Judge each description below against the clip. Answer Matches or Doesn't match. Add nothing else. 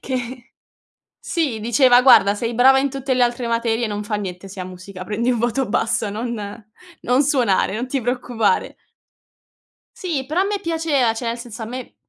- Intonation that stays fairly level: Doesn't match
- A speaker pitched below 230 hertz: Doesn't match